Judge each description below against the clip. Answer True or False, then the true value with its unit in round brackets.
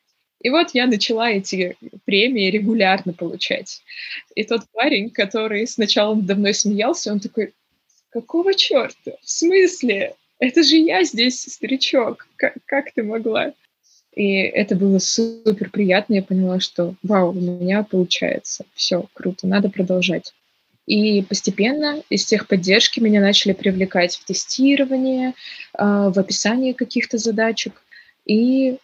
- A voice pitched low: False (215 Hz)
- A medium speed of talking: True (125 wpm)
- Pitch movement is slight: False (4.5 semitones)